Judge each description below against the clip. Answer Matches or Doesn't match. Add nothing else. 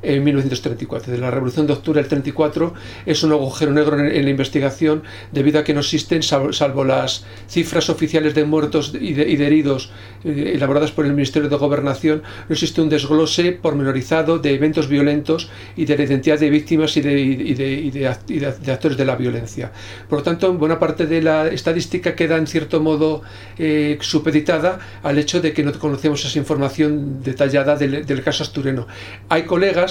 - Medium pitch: Matches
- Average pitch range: Doesn't match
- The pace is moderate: Matches